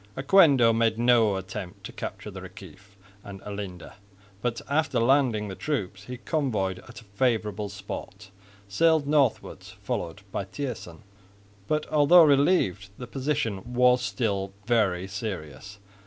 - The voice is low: Yes, low, 110 Hz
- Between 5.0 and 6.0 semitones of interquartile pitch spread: Yes, average, 5.3 semitones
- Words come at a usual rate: No, slow, 130 wpm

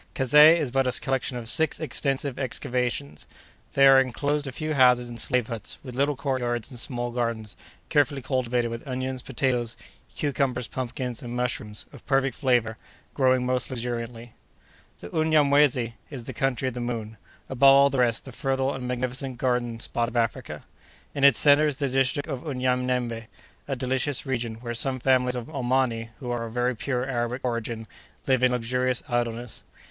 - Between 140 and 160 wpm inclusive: No, average, 170 wpm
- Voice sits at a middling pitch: No, low, 125 Hz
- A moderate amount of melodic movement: No, narrow, 2.0 semitones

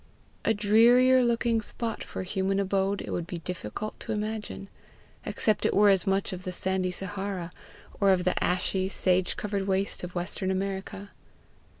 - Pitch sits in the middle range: No, high, 195 Hz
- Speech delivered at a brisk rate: No, average, 165 wpm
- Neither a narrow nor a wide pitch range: No, narrow, 2.0 semitones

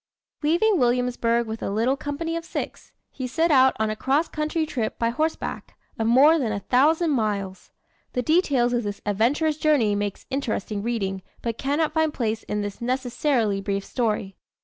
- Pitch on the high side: Yes, high, 245 Hz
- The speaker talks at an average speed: Yes, average, 170 wpm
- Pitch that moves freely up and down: Yes, wide, 5.7 semitones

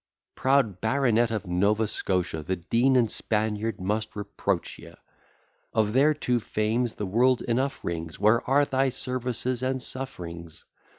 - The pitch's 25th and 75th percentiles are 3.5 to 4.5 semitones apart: Yes, average, 3.9 semitones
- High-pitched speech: No, low, 115 Hz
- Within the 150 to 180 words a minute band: No, average, 140 wpm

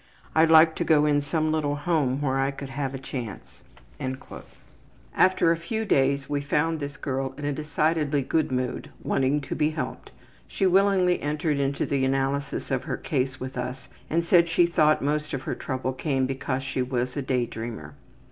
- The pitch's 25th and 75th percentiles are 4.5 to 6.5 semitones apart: No, average, 2.8 semitones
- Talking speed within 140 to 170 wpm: No, average, 185 wpm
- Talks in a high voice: No, medium, 145 Hz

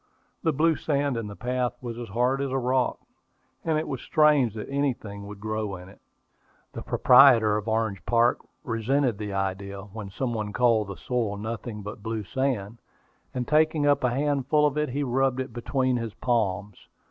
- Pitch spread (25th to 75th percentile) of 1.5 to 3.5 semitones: No, average, 4.2 semitones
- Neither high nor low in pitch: No, low, 120 Hz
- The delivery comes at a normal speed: Yes, average, 185 wpm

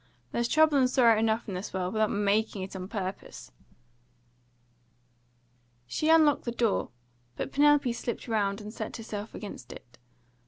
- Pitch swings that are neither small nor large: Yes, average, 3.7 semitones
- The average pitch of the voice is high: Yes, high, 220 Hz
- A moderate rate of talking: Yes, average, 150 wpm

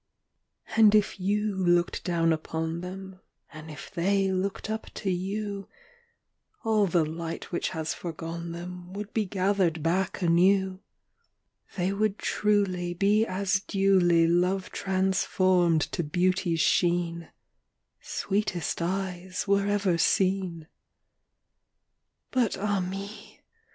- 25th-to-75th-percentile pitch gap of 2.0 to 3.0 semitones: Yes, narrow, 2.5 semitones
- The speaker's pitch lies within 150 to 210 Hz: Yes, medium, 185 Hz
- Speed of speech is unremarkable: No, slow, 120 wpm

